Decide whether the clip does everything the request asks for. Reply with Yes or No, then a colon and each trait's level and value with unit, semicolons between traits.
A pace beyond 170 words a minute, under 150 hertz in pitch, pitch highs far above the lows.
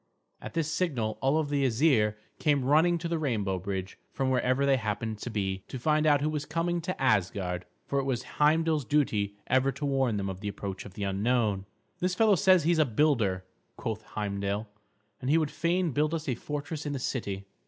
Yes: fast, 205 wpm; low, 135 Hz; wide, 6.8 semitones